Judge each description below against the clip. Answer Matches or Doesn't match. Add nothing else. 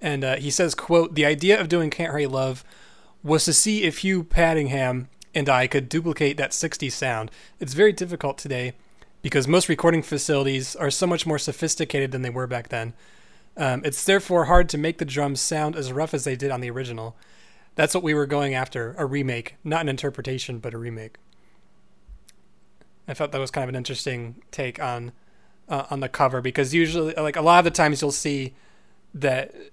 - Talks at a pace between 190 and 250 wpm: Matches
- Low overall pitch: Doesn't match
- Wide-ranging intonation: Doesn't match